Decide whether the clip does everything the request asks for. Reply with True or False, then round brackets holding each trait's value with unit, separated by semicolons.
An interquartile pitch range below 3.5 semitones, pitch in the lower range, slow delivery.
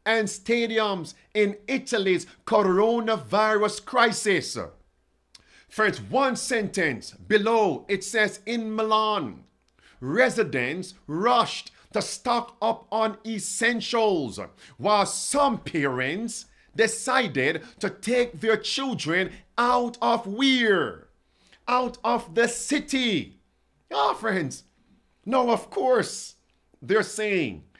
False (2.7 semitones; 220 Hz; 95 wpm)